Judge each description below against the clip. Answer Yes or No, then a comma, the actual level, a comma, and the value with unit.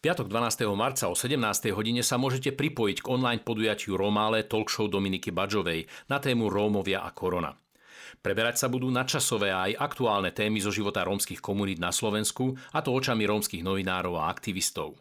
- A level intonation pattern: No, average, 4.3 semitones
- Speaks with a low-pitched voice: Yes, low, 105 Hz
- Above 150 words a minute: Yes, fast, 165 wpm